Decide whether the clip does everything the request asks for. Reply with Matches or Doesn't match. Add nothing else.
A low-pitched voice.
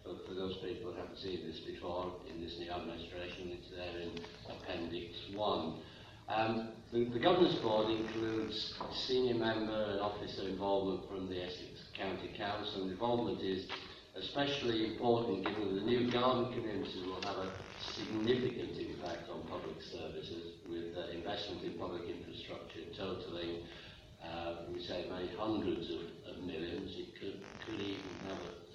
Matches